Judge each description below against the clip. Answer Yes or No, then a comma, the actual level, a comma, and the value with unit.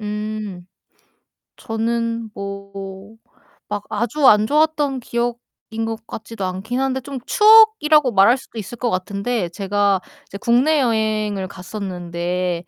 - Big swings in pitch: No, average, 3.5 semitones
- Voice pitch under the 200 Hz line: No, high, 215 Hz